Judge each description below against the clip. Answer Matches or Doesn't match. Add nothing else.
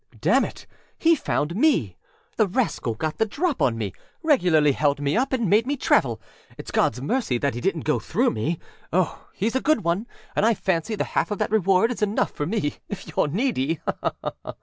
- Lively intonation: Matches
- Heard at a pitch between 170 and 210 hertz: Matches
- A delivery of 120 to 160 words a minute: Doesn't match